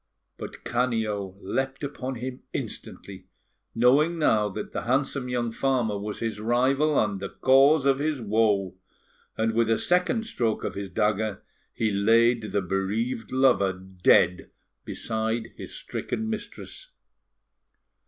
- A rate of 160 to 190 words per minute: No, slow, 135 wpm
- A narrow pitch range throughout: No, average, 4.3 semitones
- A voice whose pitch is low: Yes, low, 115 Hz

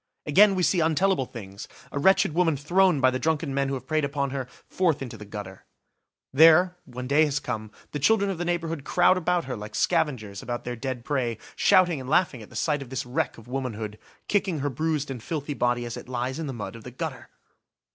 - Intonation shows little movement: No, average, 5.0 semitones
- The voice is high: No, medium, 140 Hz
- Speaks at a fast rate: Yes, fast, 220 wpm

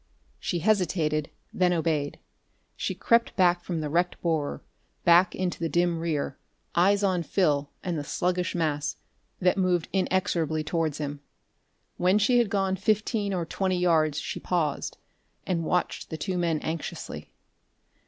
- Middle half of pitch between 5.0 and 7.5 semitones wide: No, average, 2.9 semitones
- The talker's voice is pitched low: No, medium, 175 Hz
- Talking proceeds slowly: No, average, 145 wpm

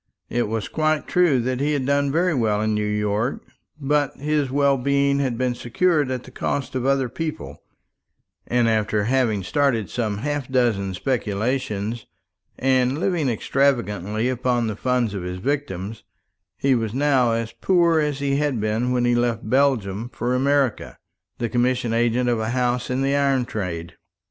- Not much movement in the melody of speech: No, average, 3.9 semitones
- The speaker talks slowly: No, average, 170 wpm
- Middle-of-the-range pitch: No, low, 125 Hz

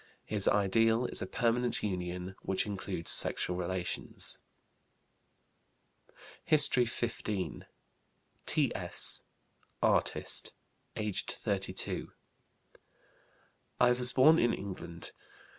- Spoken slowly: Yes, slow, 80 wpm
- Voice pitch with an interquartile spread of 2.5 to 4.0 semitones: No, average, 4.8 semitones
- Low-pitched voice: Yes, low, 105 Hz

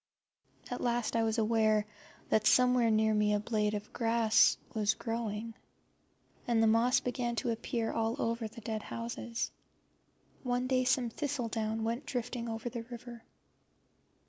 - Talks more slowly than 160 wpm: Yes, average, 145 wpm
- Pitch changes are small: Yes, narrow, 1.7 semitones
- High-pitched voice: Yes, high, 230 Hz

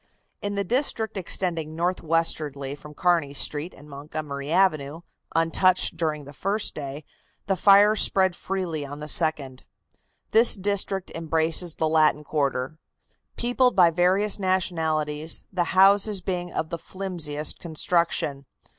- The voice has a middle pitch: Yes, medium, 165 Hz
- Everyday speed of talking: No, slow, 130 wpm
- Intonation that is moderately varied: Yes, average, 3.9 semitones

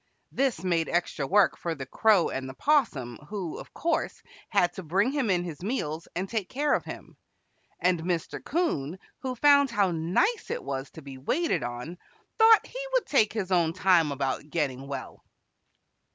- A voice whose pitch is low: No, medium, 180 Hz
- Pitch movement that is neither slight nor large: No, wide, 8.5 semitones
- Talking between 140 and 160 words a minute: No, average, 180 wpm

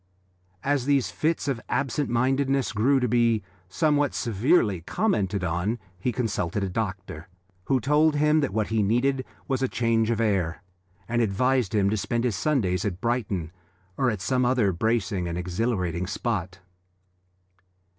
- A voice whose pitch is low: Yes, low, 115 Hz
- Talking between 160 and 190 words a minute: No, average, 150 wpm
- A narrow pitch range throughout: No, average, 5.2 semitones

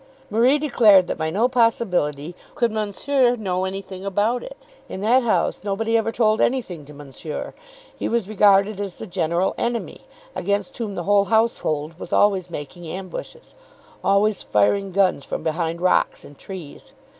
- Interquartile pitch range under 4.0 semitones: No, average, 4.3 semitones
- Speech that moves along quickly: No, average, 155 wpm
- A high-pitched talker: Yes, high, 200 Hz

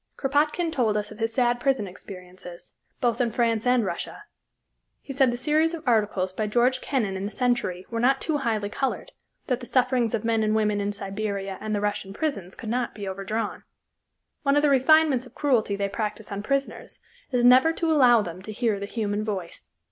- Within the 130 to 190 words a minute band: No, average, 200 wpm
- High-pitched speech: Yes, high, 225 Hz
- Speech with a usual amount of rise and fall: Yes, average, 4.2 semitones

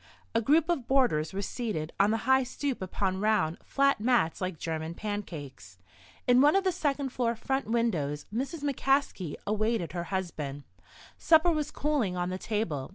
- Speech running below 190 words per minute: Yes, average, 165 wpm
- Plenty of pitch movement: Yes, wide, 7.7 semitones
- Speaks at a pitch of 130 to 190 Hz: No, high, 220 Hz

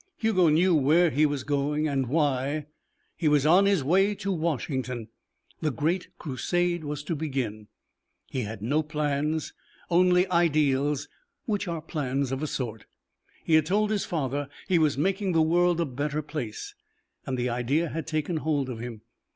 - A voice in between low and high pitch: Yes, medium, 150 Hz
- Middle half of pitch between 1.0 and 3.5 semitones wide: No, average, 4.0 semitones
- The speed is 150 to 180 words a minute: Yes, average, 165 wpm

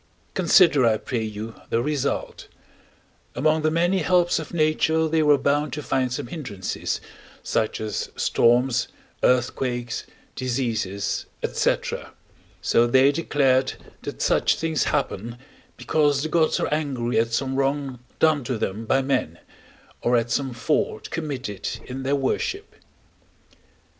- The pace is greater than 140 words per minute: No, slow, 135 wpm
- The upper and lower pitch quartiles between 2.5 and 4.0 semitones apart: No, average, 4.4 semitones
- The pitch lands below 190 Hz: Yes, low, 135 Hz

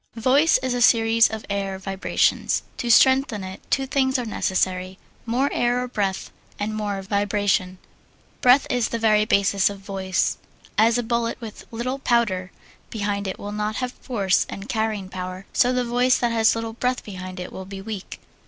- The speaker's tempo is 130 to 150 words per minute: No, average, 180 wpm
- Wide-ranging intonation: No, average, 3.8 semitones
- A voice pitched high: Yes, high, 215 Hz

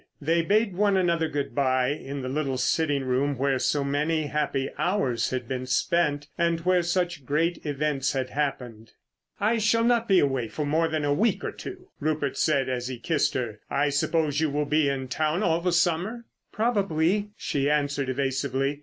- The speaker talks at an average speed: Yes, average, 180 wpm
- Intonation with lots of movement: No, average, 3.9 semitones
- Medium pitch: Yes, medium, 150 Hz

